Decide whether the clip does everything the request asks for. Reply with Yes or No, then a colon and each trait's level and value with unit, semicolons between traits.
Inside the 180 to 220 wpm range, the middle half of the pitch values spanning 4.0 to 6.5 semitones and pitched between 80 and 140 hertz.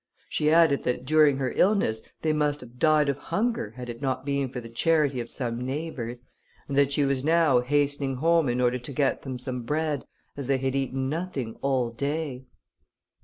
No: average, 195 wpm; average, 3.3 semitones; low, 135 Hz